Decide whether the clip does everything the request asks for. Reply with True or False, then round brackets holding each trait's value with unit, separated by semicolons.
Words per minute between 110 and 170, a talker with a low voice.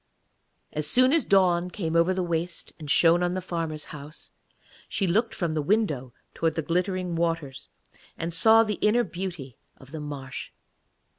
False (165 wpm; 170 Hz)